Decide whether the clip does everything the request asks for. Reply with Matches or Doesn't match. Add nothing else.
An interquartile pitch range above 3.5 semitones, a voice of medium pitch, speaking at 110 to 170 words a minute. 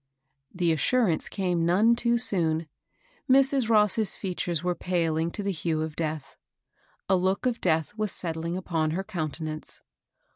Matches